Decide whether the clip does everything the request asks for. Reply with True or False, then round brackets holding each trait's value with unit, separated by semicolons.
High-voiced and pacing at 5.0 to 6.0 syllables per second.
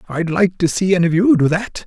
False (180 Hz; 5.9 syllables/s)